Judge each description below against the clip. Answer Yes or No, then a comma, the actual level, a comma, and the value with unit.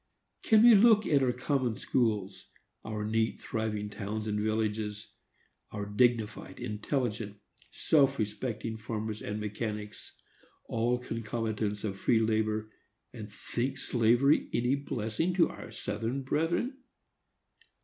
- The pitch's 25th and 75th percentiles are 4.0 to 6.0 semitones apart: No, average, 3.2 semitones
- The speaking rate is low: Yes, slow, 120 wpm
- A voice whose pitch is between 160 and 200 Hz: No, low, 110 Hz